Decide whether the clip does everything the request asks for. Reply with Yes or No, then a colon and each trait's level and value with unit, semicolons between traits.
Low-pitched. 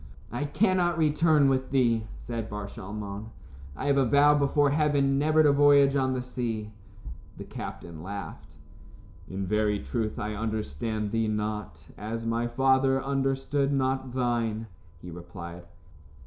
Yes: low, 120 Hz